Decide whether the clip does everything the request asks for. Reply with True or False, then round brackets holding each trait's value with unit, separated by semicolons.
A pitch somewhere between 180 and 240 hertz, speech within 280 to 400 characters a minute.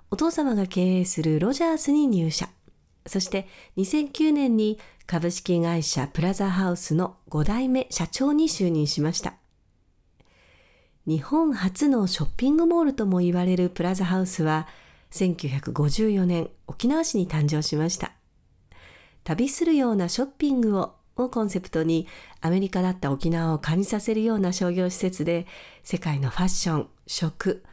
True (185 Hz; 290 characters per minute)